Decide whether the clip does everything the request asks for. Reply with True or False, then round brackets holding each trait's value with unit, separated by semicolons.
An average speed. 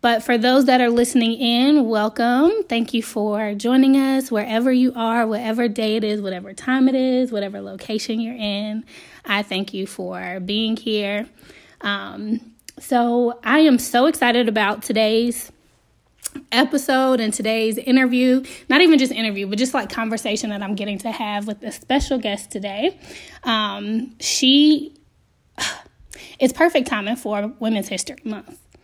True (150 wpm)